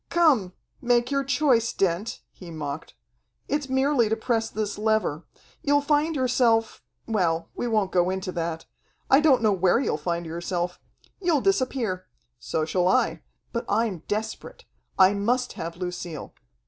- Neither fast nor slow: Yes, average, 150 wpm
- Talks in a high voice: Yes, high, 215 Hz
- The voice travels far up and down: Yes, wide, 6.3 semitones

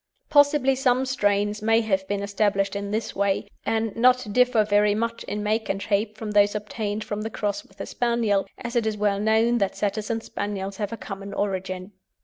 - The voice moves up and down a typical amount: No, narrow, 2.2 semitones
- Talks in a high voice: Yes, high, 210 Hz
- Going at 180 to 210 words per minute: Yes, average, 200 wpm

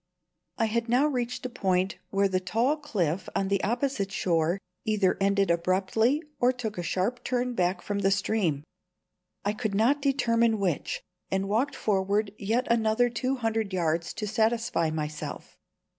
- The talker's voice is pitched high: Yes, high, 210 Hz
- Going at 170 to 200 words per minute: No, average, 160 wpm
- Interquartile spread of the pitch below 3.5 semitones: No, average, 4.0 semitones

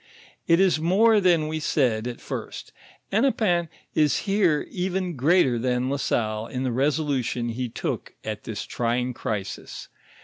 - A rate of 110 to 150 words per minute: Yes, average, 145 wpm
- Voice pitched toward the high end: No, medium, 145 Hz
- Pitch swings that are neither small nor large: No, wide, 6.3 semitones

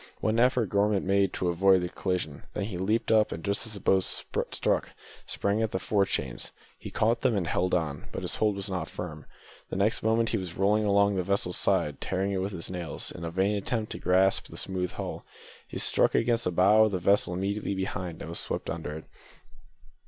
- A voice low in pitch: Yes, very low, 95 Hz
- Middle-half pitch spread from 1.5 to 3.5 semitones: Yes, average, 2.7 semitones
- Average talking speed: No, fast, 220 wpm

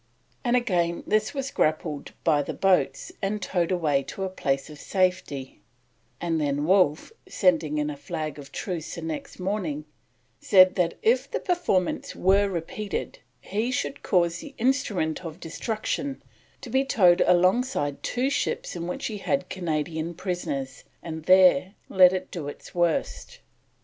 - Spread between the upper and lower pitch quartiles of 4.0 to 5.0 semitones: Yes, average, 4.3 semitones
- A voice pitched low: No, medium, 180 Hz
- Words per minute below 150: No, average, 155 wpm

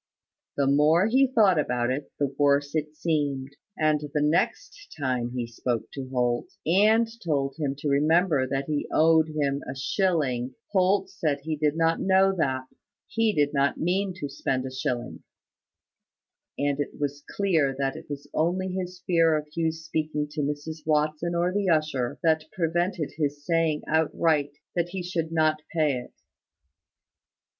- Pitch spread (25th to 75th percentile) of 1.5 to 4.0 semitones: Yes, average, 3.3 semitones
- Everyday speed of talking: Yes, average, 160 wpm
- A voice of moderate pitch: Yes, medium, 155 Hz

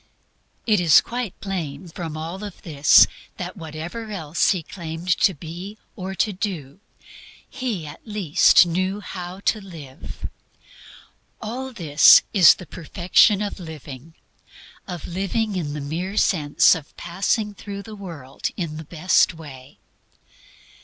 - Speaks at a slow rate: Yes, slow, 130 wpm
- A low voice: No, medium, 175 Hz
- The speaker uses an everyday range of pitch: Yes, average, 4.1 semitones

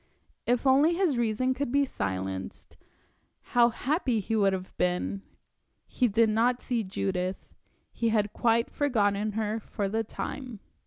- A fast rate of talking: No, average, 145 wpm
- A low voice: No, high, 225 Hz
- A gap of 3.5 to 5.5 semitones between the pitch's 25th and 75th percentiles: Yes, average, 3.9 semitones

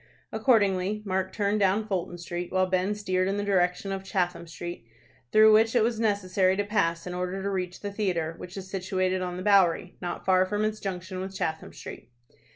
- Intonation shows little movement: Yes, narrow, 2.1 semitones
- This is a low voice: No, high, 190 Hz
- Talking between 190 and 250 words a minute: Yes, average, 200 wpm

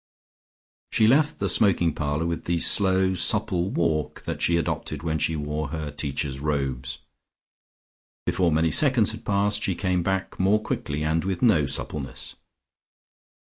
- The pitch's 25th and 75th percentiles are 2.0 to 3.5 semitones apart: No, average, 4.4 semitones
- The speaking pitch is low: Yes, very low, 85 Hz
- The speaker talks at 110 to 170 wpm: Yes, average, 145 wpm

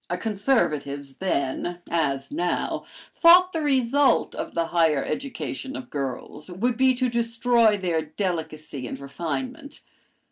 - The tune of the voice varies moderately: No, wide, 9.0 semitones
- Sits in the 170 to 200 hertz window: Yes, medium, 185 Hz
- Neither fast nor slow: No, slow, 120 wpm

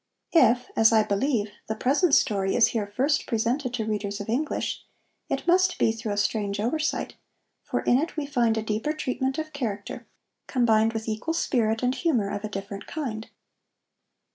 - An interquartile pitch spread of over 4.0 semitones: Yes, average, 4.7 semitones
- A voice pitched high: Yes, high, 225 Hz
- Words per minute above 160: Yes, average, 175 wpm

